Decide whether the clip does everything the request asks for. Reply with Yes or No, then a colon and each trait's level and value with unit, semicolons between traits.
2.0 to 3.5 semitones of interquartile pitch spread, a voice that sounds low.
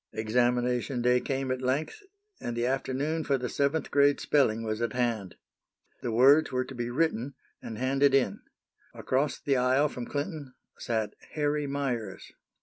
Yes: average, 2.8 semitones; low, 130 Hz